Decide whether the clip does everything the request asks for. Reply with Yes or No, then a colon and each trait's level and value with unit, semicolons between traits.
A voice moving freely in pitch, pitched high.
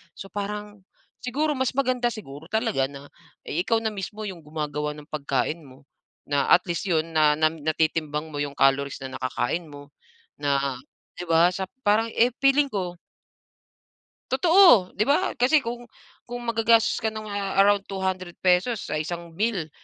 No: wide, 6.8 semitones; medium, 180 Hz